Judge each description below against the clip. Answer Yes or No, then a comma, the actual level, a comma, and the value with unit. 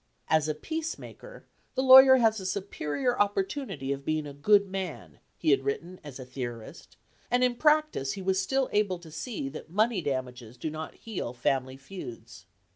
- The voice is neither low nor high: Yes, medium, 180 Hz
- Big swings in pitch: Yes, wide, 8.6 semitones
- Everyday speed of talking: Yes, average, 175 wpm